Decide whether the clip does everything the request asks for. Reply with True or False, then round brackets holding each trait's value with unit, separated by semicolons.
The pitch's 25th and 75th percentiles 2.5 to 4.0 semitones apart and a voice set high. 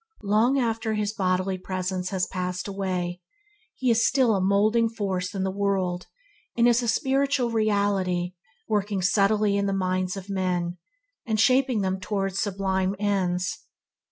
True (2.8 semitones; 195 Hz)